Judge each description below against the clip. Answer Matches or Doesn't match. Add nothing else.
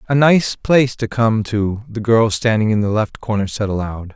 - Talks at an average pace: Doesn't match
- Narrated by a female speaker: Doesn't match